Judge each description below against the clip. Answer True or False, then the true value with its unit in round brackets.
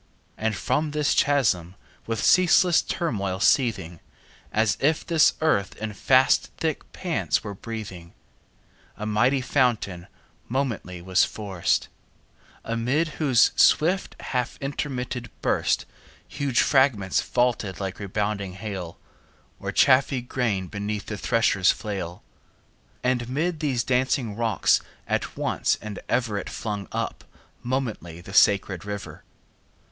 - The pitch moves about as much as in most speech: True (5.0 semitones)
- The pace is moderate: False (120 wpm)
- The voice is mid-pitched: False (115 Hz)